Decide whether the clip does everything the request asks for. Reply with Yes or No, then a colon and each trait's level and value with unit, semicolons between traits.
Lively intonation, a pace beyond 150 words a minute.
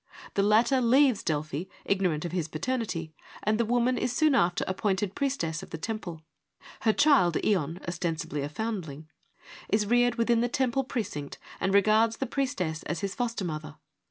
Yes: wide, 6.5 semitones; average, 165 wpm